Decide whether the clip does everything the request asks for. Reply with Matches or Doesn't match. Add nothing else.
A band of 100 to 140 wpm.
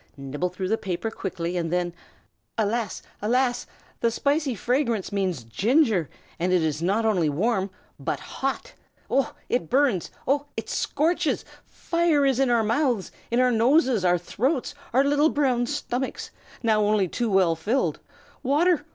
Doesn't match